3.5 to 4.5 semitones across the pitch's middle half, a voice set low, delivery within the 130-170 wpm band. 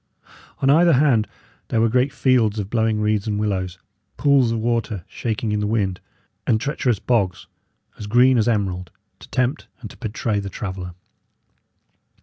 No: average, 3.1 semitones; low, 110 Hz; average, 160 wpm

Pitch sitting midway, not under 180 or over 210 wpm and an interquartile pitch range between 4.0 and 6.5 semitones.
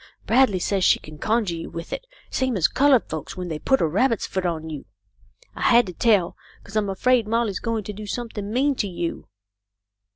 No: high, 205 Hz; fast, 205 wpm; average, 5.3 semitones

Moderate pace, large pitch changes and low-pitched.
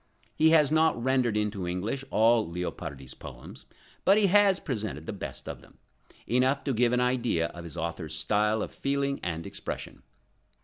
Yes: average, 170 wpm; wide, 7.8 semitones; low, 115 Hz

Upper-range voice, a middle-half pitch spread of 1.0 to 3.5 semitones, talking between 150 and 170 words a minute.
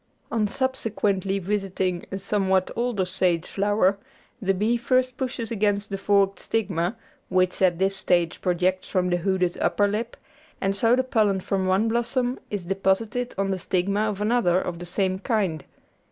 Yes: high, 195 Hz; average, 2.9 semitones; average, 165 wpm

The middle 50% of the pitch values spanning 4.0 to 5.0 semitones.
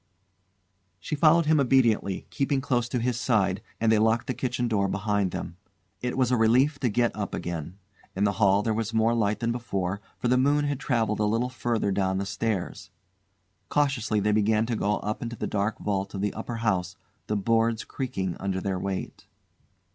No: average, 3.6 semitones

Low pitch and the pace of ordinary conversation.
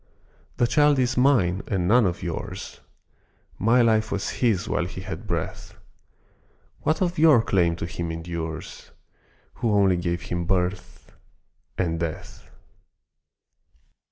No: very low, 95 Hz; slow, 130 wpm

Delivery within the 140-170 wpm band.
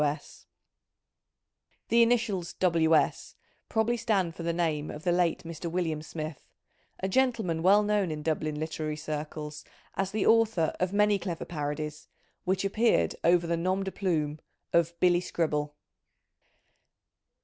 Yes: average, 150 wpm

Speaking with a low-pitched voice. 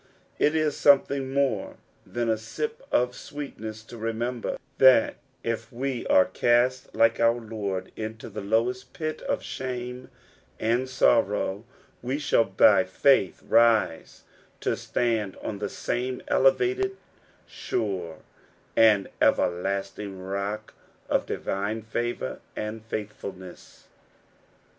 Yes: low, 115 Hz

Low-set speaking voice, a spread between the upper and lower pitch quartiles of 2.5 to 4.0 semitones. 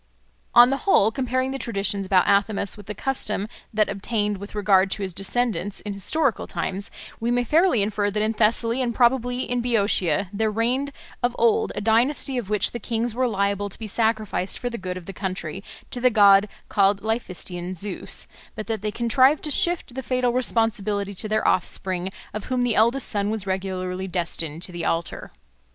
No: high, 215 Hz; average, 3.6 semitones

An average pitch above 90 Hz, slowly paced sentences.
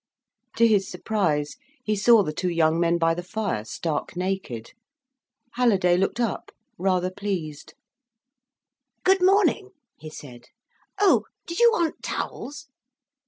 Yes: high, 190 Hz; slow, 120 wpm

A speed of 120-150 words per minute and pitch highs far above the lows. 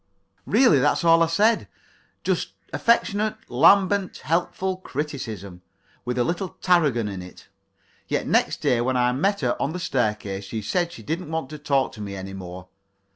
No: average, 170 wpm; wide, 8.3 semitones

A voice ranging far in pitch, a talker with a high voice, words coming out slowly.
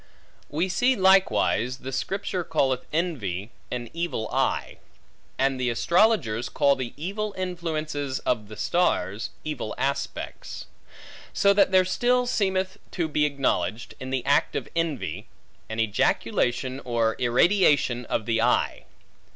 No: wide, 7.2 semitones; medium, 140 Hz; slow, 130 wpm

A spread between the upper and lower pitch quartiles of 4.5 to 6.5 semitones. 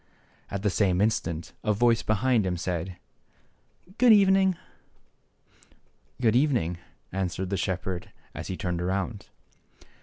Yes: average, 5.0 semitones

